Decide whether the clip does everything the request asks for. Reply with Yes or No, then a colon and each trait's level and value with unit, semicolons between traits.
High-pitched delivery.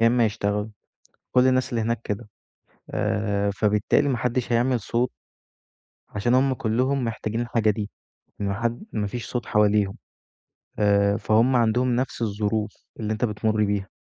No: low, 110 Hz